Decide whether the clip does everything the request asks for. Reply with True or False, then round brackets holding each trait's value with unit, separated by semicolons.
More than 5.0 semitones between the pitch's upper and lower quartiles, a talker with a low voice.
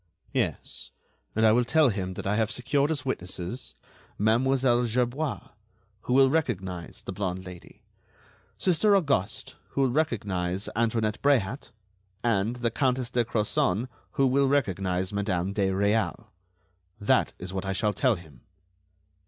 True (5.4 semitones; 110 Hz)